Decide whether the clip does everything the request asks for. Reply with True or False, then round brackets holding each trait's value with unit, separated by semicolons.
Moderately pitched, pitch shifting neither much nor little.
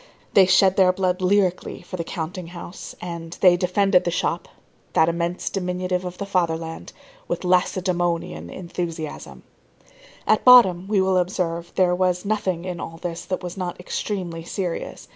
False (180 Hz; 1.6 semitones)